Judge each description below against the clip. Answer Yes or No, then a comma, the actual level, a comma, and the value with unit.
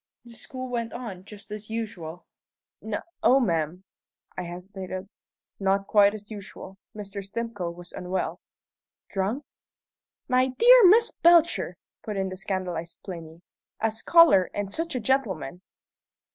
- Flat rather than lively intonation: No, average, 4.5 semitones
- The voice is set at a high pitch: Yes, high, 205 Hz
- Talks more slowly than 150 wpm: Yes, average, 140 wpm